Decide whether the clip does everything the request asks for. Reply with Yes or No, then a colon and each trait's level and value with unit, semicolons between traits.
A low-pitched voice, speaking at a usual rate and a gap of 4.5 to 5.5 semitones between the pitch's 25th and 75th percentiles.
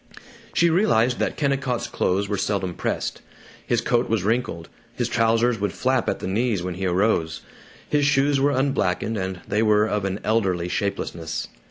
Yes: low, 110 Hz; average, 170 wpm; average, 4.9 semitones